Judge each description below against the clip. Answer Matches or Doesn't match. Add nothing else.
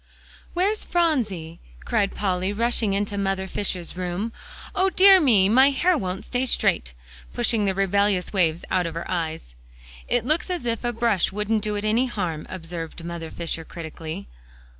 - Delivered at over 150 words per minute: Matches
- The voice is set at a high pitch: Matches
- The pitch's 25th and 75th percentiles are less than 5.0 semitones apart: Doesn't match